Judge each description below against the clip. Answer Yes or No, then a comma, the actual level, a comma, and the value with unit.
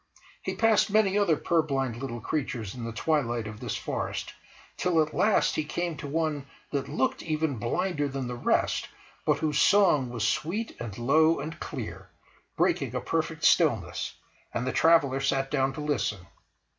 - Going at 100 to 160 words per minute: No, average, 170 wpm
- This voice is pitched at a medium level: Yes, medium, 145 Hz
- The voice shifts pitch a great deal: No, average, 4.7 semitones